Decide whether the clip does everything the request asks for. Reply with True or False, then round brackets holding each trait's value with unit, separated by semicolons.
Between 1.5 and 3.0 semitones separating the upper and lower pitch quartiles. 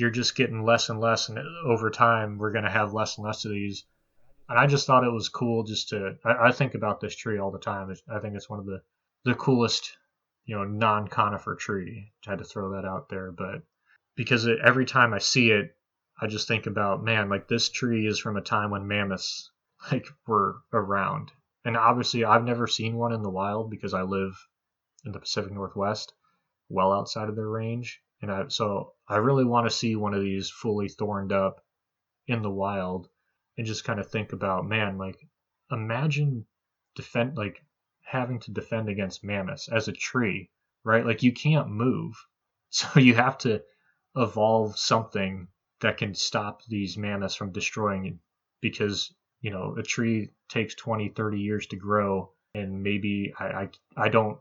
True (2.6 semitones)